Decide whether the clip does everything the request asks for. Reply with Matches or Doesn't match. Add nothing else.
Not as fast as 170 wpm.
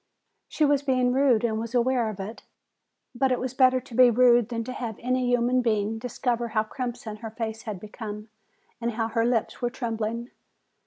Doesn't match